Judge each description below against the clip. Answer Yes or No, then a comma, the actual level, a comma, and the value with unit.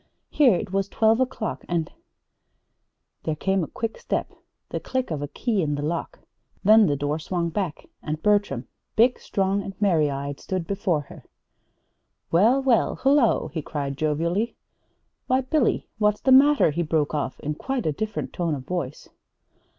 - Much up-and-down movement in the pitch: Yes, wide, 6.4 semitones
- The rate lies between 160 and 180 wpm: Yes, average, 165 wpm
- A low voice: No, medium, 185 Hz